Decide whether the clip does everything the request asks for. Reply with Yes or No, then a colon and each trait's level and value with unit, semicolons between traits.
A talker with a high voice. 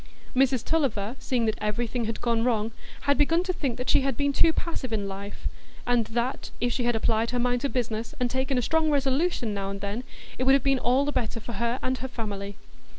Yes: high, 245 Hz